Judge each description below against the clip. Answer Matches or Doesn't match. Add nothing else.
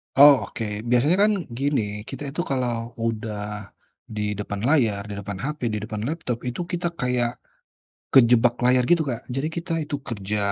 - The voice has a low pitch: Matches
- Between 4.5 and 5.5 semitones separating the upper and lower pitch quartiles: Matches